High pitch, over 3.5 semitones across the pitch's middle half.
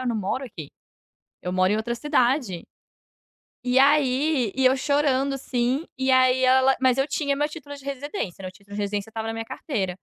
Yes: very high, 255 Hz; average, 4.1 semitones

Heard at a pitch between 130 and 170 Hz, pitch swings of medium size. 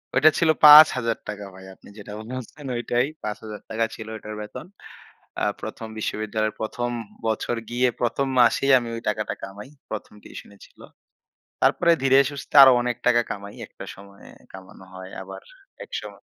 No: low, 110 Hz; average, 3.3 semitones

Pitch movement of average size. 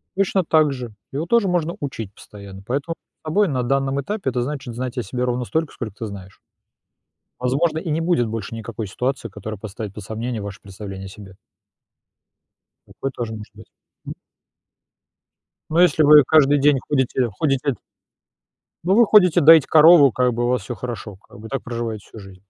No: wide, 5.7 semitones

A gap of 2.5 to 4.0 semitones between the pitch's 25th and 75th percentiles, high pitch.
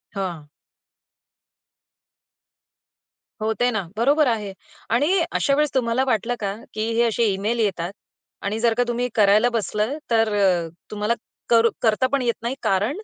Yes: average, 2.9 semitones; high, 225 Hz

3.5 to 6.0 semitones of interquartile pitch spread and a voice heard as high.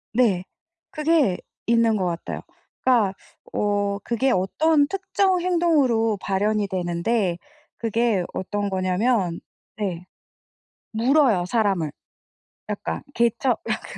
Yes: average, 5.1 semitones; high, 220 Hz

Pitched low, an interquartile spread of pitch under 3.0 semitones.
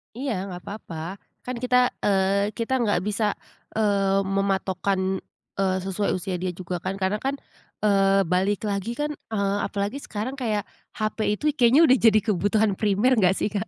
No: high, 200 Hz; narrow, 2.4 semitones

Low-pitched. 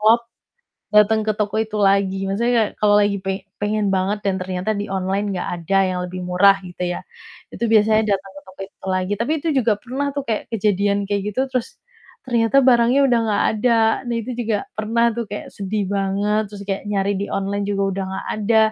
No: high, 205 Hz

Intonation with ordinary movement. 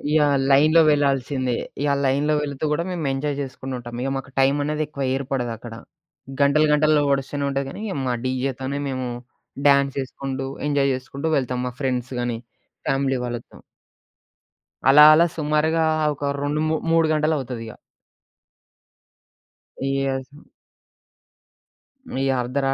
No: narrow, 2.1 semitones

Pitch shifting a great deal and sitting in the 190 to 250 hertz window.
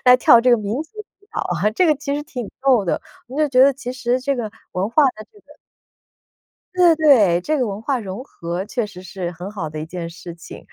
Yes: wide, 6.7 semitones; high, 235 Hz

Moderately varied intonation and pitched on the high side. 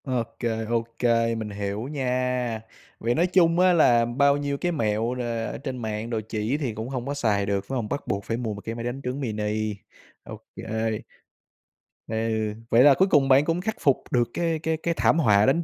No: average, 4.3 semitones; low, 125 Hz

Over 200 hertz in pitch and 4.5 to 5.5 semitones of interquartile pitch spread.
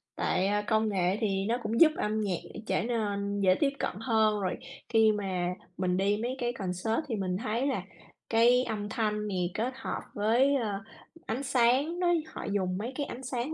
No: high, 215 Hz; average, 3.5 semitones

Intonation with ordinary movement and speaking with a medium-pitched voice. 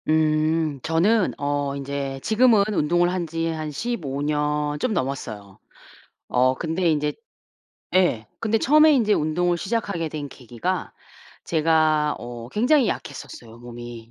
Yes: average, 4.4 semitones; medium, 155 Hz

